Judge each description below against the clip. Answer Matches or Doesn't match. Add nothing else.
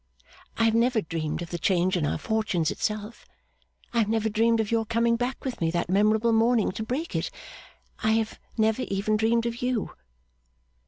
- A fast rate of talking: Doesn't match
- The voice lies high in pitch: Matches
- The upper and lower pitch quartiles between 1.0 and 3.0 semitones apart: Matches